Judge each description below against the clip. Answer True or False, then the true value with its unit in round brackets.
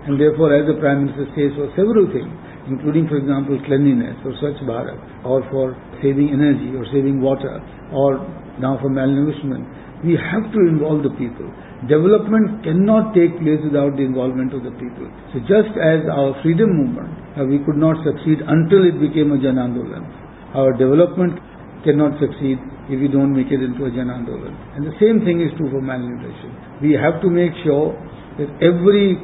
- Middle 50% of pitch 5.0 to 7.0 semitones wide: False (3.2 semitones)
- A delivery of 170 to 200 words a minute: True (180 wpm)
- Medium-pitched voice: True (145 Hz)